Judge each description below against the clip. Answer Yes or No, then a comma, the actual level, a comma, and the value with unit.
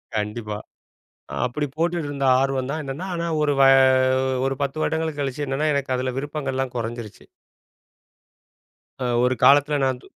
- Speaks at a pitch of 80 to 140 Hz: Yes, low, 135 Hz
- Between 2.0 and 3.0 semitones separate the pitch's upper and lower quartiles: Yes, narrow, 2.6 semitones